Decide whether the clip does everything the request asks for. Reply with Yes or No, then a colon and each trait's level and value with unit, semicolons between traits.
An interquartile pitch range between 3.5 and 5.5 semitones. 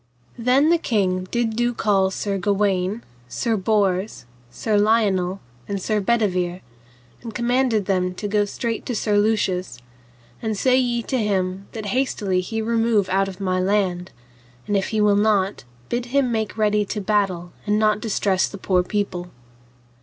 No: average, 2.9 semitones